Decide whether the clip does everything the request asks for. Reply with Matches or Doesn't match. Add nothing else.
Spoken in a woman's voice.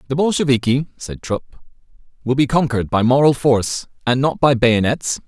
Doesn't match